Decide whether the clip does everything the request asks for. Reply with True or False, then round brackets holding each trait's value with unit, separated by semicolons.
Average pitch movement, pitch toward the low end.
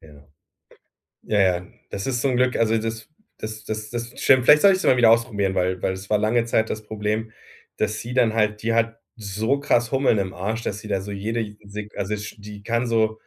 False (2.2 semitones; 110 Hz)